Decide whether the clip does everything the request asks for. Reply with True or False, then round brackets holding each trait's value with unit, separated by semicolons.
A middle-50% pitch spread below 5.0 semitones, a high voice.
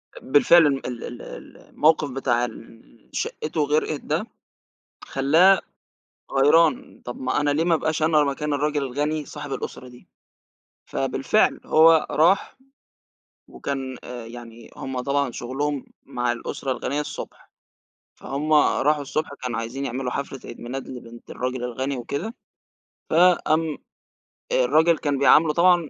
False (3.5 semitones; 140 Hz)